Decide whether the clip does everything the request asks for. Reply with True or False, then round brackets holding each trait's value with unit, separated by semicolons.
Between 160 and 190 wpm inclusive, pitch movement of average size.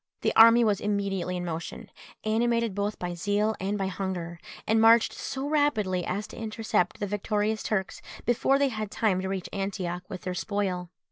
True (180 wpm; 3.0 semitones)